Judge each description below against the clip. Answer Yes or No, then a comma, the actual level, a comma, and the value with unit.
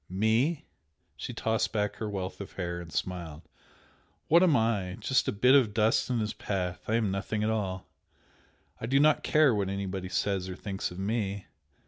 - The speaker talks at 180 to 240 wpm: Yes, average, 185 wpm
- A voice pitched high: No, low, 105 Hz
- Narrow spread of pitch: No, average, 3.3 semitones